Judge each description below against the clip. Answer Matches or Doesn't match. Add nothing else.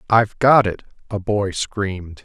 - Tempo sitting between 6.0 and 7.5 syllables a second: Doesn't match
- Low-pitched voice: Matches